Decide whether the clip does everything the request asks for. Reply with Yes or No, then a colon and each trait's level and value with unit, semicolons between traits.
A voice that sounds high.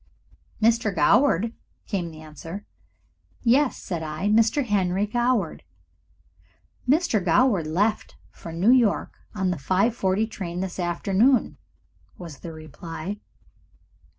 Yes: high, 195 Hz